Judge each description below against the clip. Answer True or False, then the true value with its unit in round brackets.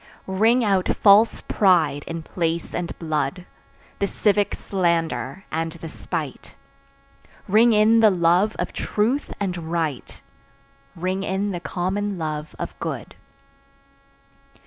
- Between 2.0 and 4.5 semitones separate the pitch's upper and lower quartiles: True (3.9 semitones)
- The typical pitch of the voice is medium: True (180 Hz)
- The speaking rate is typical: False (120 wpm)